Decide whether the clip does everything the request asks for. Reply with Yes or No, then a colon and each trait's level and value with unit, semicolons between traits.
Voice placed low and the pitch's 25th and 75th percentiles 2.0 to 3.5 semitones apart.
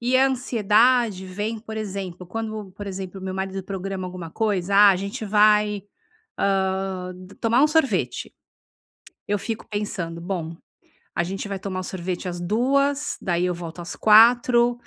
No: high, 200 Hz; average, 3.2 semitones